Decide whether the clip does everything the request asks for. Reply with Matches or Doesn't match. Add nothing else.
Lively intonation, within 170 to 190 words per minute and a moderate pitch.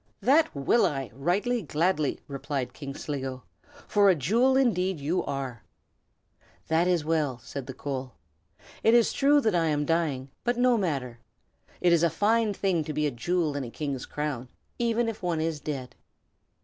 Matches